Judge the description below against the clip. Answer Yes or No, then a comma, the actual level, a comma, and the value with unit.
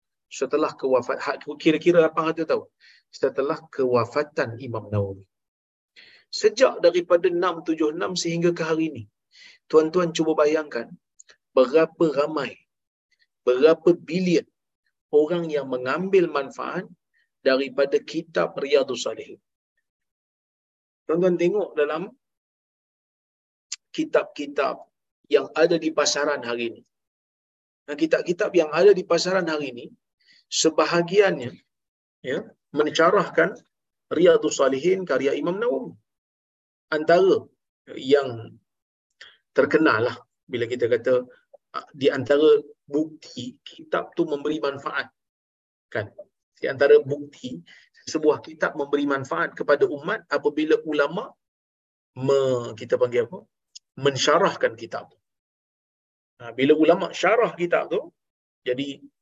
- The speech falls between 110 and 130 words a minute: No, average, 95 wpm